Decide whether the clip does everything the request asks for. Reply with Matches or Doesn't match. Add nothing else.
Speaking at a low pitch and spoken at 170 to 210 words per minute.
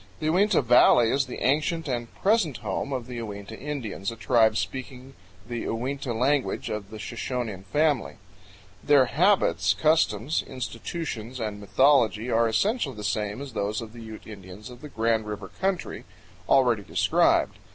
Doesn't match